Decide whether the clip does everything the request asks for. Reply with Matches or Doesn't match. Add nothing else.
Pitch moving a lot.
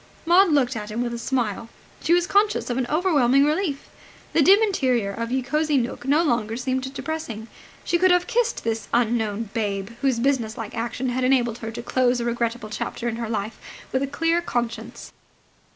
Doesn't match